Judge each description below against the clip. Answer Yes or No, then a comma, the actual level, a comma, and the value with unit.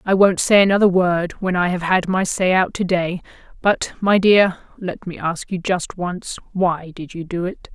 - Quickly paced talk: Yes, fast, 210 wpm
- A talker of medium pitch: Yes, medium, 180 Hz